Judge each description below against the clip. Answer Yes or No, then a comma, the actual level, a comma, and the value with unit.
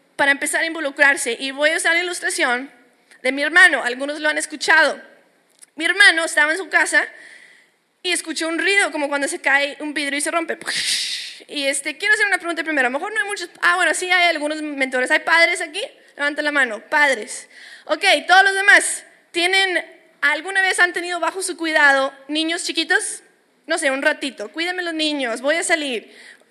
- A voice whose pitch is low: No, very high, 320 Hz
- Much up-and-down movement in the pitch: No, average, 3.5 semitones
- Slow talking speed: No, average, 195 wpm